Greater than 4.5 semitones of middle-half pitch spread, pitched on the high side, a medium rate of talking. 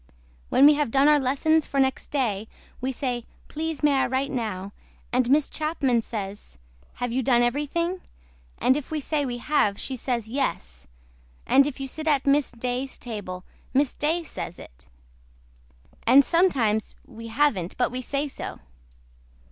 No: average, 3.9 semitones; very high, 265 Hz; average, 165 wpm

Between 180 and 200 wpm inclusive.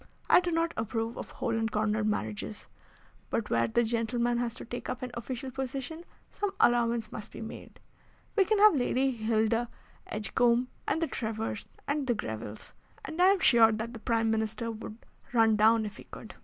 Yes: average, 185 wpm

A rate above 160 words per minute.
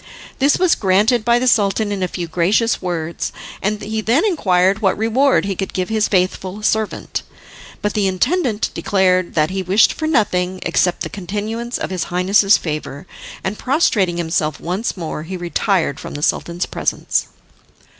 Yes: average, 170 wpm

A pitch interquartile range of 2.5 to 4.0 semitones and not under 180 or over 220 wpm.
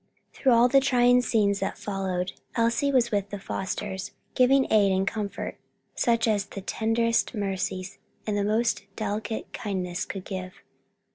No: average, 3.3 semitones; average, 145 wpm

